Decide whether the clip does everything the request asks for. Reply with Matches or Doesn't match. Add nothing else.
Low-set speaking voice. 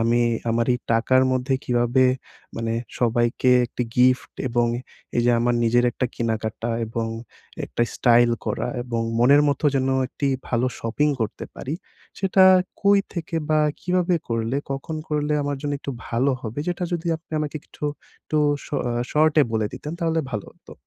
Matches